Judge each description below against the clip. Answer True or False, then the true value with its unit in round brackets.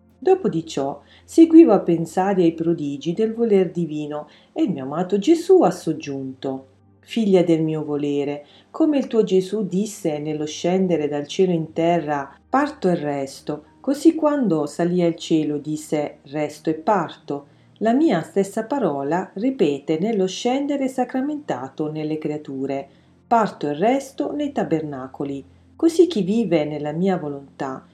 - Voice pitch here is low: False (170 Hz)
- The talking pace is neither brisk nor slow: True (140 wpm)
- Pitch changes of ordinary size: False (6.8 semitones)